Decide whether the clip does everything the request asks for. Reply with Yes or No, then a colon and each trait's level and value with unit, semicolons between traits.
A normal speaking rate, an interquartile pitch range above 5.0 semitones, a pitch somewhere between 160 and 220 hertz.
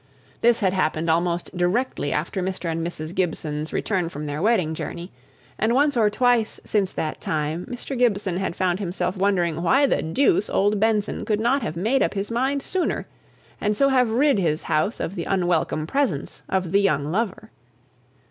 Yes: average, 180 wpm; wide, 5.5 semitones; high, 190 Hz